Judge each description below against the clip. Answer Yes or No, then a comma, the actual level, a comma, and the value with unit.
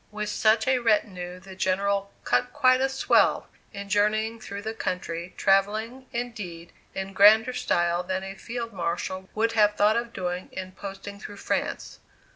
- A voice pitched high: Yes, high, 200 Hz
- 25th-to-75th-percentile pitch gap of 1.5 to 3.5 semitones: Yes, average, 3.0 semitones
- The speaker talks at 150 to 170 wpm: Yes, average, 160 wpm